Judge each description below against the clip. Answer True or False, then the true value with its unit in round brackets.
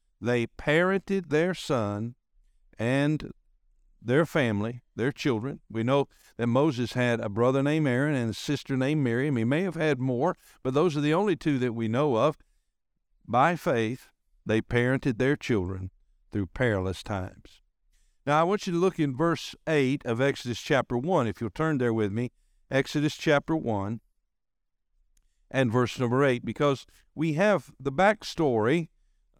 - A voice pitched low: True (130 Hz)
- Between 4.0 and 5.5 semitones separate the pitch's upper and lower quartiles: True (4.8 semitones)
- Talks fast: False (160 wpm)